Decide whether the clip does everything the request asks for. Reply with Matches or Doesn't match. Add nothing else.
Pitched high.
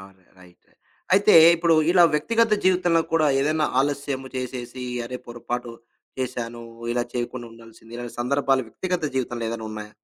Doesn't match